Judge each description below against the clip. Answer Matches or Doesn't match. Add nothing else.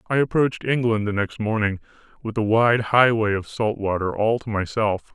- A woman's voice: Doesn't match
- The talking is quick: Doesn't match